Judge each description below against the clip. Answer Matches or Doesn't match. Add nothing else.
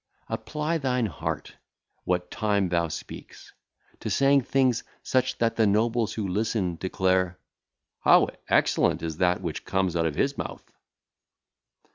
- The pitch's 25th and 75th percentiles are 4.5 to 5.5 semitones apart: Matches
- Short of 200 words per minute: Matches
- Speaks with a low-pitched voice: Matches